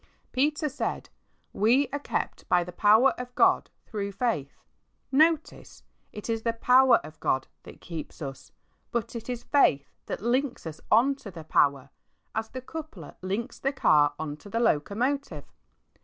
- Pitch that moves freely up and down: Yes, wide, 8.0 semitones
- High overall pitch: Yes, high, 225 Hz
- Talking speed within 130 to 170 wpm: Yes, average, 165 wpm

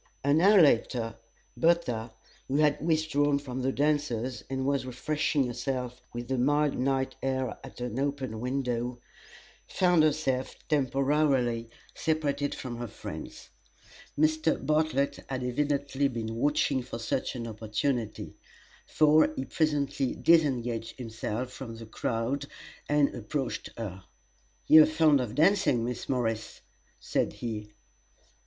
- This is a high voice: No, low, 135 Hz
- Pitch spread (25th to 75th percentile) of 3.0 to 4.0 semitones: Yes, average, 3.6 semitones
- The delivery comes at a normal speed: No, slow, 125 wpm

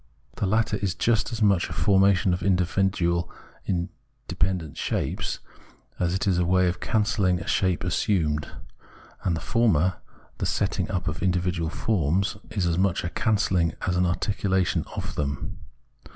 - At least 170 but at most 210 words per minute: No, average, 150 wpm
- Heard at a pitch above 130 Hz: No, very low, 90 Hz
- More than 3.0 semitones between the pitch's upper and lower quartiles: No, narrow, 2.4 semitones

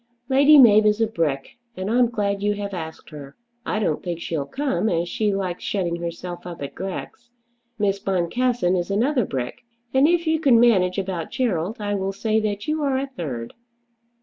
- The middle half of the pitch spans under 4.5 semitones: No, wide, 5.5 semitones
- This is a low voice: No, high, 200 Hz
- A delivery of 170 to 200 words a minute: Yes, average, 190 wpm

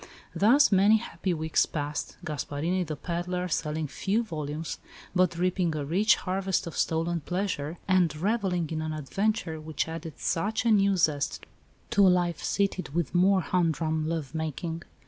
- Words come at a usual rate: Yes, average, 155 wpm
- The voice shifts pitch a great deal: No, average, 3.2 semitones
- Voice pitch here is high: No, medium, 170 Hz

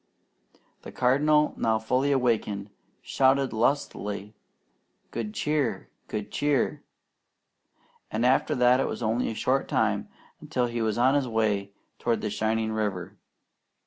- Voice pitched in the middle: No, low, 120 Hz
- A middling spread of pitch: Yes, average, 3.4 semitones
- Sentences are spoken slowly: Yes, slow, 130 wpm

